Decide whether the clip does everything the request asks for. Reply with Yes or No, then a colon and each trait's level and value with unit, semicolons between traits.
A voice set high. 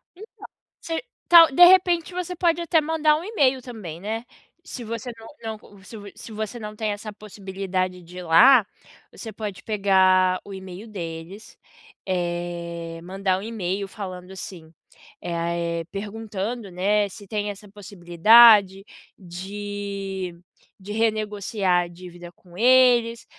Yes: high, 205 Hz